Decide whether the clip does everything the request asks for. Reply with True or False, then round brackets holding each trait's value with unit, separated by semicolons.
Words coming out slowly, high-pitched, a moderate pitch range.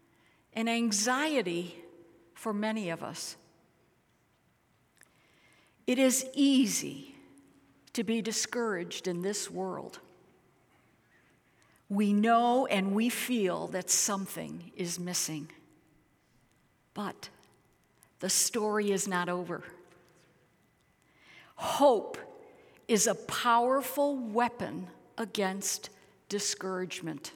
True (80 wpm; 205 Hz; 4.8 semitones)